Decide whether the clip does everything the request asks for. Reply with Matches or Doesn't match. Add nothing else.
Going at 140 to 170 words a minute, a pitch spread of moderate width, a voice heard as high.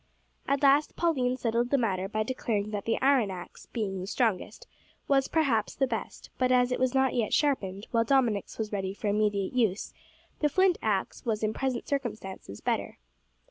Doesn't match